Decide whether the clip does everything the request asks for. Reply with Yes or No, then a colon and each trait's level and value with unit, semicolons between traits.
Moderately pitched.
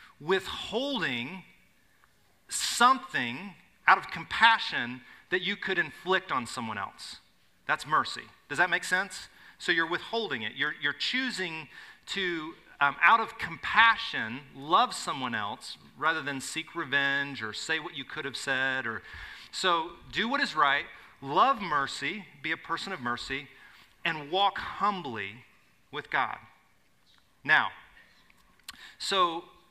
Yes: medium, 175 Hz